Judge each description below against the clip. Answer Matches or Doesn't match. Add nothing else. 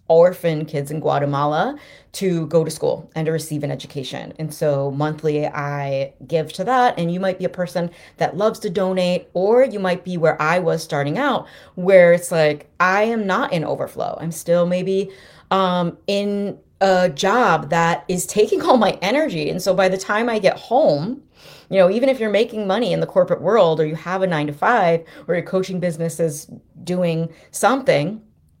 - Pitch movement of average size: Matches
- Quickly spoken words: Doesn't match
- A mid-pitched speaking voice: Matches